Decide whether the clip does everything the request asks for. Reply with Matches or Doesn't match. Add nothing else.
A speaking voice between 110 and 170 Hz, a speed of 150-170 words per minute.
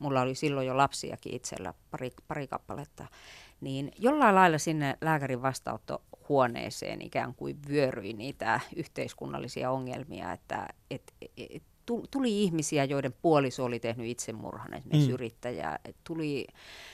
Doesn't match